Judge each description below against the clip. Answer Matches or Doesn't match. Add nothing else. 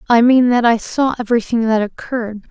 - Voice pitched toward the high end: Matches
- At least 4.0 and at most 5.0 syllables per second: Doesn't match